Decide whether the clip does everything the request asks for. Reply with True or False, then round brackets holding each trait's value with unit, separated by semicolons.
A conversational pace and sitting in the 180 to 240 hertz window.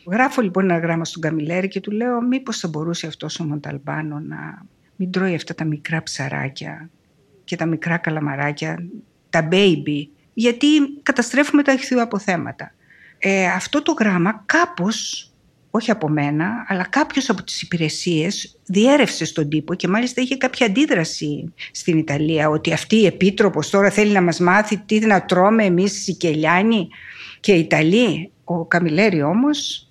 True (155 wpm; 185 Hz)